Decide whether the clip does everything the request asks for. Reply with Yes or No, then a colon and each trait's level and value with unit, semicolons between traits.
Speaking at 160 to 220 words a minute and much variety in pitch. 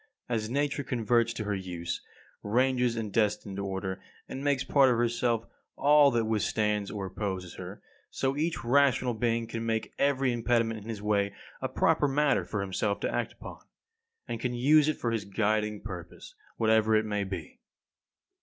No: average, 170 wpm; average, 3.5 semitones